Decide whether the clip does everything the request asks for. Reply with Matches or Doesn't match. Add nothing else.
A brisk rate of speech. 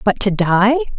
Doesn't match